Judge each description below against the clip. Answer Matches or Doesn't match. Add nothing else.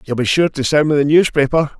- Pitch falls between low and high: Matches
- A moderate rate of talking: Doesn't match